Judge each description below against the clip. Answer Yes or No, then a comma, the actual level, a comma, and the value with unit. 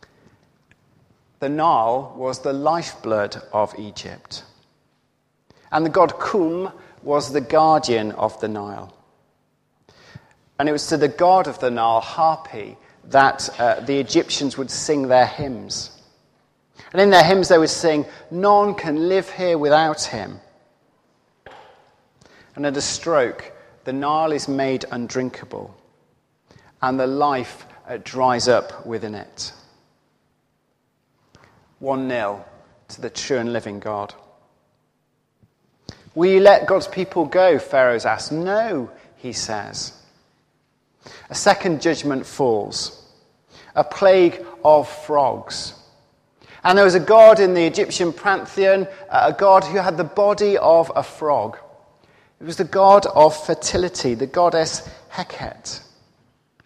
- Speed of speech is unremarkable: No, slow, 125 wpm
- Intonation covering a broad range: Yes, wide, 5.7 semitones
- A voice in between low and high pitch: Yes, medium, 150 Hz